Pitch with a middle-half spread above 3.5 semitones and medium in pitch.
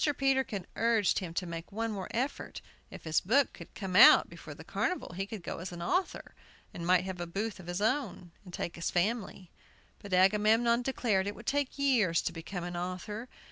No: average, 4.7 semitones; high, 195 Hz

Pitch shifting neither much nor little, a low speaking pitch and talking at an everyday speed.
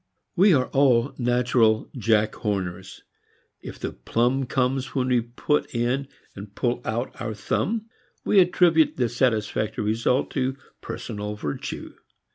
No: average, 3.5 semitones; low, 120 Hz; slow, 130 wpm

